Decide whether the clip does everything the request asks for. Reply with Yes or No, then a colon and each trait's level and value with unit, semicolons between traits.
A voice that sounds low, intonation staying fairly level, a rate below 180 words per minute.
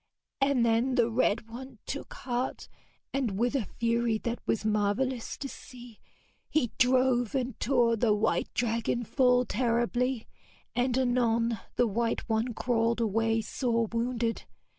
No: high, 235 Hz; narrow, 1.8 semitones; average, 140 wpm